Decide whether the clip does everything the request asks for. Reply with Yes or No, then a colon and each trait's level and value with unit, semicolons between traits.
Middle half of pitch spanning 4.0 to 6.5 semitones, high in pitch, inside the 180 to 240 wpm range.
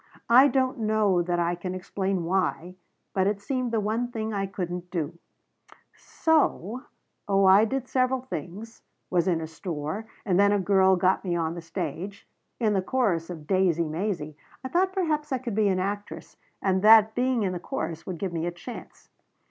Yes: average, 4.3 semitones; high, 195 Hz; average, 190 wpm